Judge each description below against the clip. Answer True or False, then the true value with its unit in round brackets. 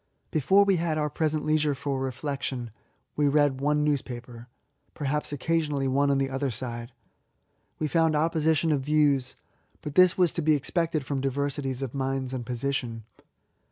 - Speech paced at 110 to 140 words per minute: False (160 wpm)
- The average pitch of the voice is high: False (140 Hz)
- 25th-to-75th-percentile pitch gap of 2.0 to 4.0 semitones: True (2.4 semitones)